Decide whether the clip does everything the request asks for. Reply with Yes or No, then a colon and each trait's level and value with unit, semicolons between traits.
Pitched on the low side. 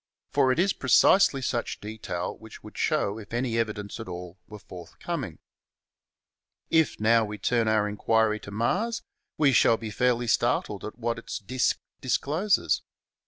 Yes: low, 115 Hz